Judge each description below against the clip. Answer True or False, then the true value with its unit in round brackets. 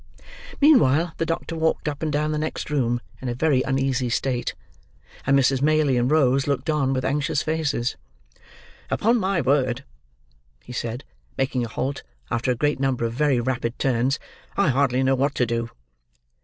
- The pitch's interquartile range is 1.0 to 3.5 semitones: True (3.2 semitones)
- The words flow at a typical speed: True (170 wpm)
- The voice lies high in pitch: False (135 Hz)